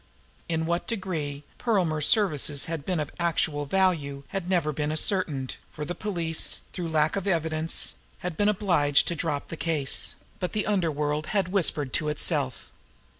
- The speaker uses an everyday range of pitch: Yes, average, 3.7 semitones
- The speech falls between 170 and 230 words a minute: No, average, 160 wpm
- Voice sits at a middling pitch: Yes, medium, 160 Hz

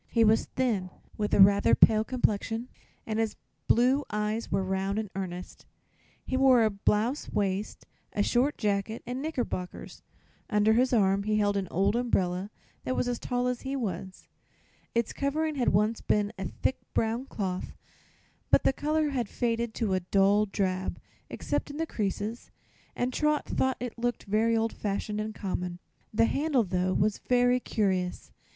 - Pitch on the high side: Yes, high, 220 Hz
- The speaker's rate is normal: Yes, average, 165 wpm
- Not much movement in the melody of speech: No, average, 3.8 semitones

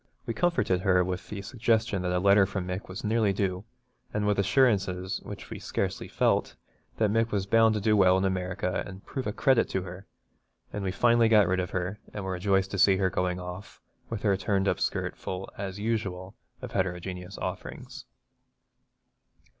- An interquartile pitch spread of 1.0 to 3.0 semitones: Yes, narrow, 2.4 semitones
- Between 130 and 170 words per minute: No, average, 190 wpm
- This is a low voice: Yes, very low, 95 Hz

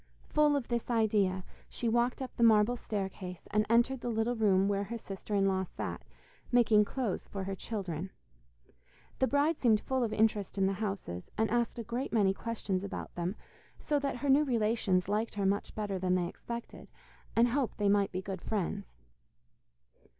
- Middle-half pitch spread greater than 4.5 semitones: No, average, 3.5 semitones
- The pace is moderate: Yes, average, 185 wpm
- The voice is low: No, high, 215 Hz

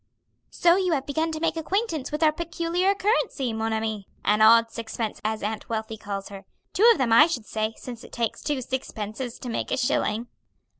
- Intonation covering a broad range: Yes, wide, 6.6 semitones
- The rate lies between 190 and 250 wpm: Yes, average, 200 wpm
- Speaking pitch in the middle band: No, high, 245 Hz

